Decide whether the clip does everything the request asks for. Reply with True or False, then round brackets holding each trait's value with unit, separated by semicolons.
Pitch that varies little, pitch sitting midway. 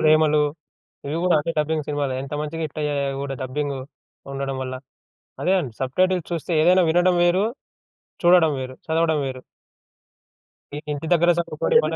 False (3.5 semitones; 155 Hz)